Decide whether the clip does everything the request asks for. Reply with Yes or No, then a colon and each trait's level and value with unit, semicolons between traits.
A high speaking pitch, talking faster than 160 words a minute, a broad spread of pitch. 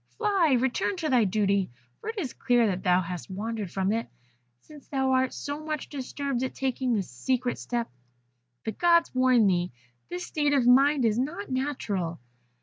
Yes: very high, 255 Hz; average, 175 wpm; wide, 5.7 semitones